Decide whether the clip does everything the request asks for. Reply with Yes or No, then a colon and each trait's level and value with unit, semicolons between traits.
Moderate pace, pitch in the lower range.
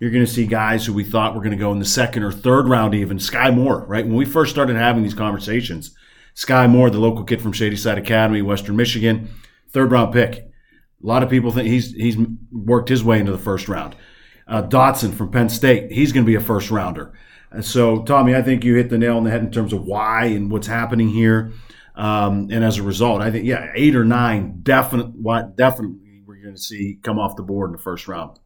No: fast, 240 wpm; low, 115 Hz